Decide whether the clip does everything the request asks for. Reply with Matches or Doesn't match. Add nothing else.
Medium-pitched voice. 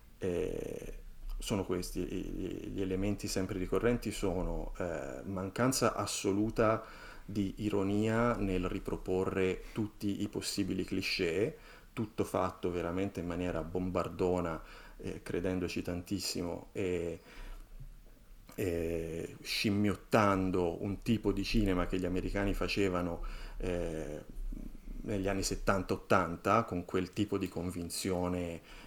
Doesn't match